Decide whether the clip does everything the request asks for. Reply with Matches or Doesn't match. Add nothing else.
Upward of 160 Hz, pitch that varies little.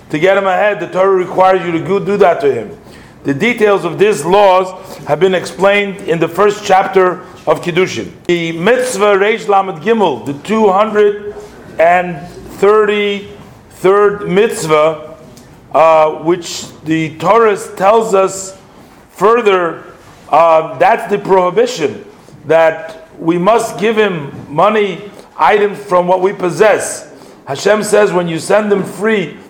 Doesn't match